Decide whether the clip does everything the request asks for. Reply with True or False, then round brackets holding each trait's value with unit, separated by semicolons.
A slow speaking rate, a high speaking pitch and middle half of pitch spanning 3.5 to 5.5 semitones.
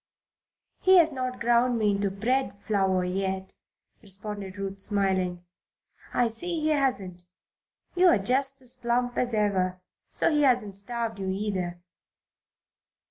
True (130 wpm; 210 Hz; 4.7 semitones)